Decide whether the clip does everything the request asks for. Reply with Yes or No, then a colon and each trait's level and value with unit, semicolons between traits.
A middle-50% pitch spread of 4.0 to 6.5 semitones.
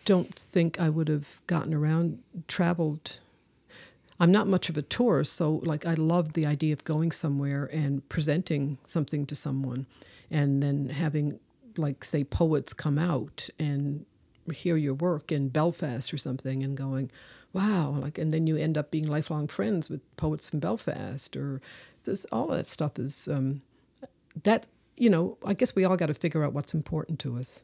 No: average, 3.0 semitones